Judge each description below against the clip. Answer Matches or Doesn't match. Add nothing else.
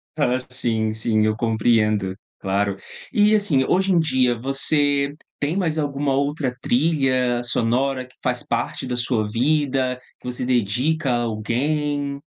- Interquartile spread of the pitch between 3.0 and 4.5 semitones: Matches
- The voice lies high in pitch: Doesn't match